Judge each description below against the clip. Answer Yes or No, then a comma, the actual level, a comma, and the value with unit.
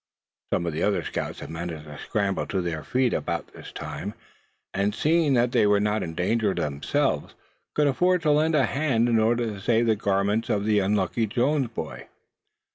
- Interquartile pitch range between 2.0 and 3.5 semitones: No, average, 4.4 semitones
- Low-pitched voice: Yes, low, 110 Hz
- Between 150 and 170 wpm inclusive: No, average, 195 wpm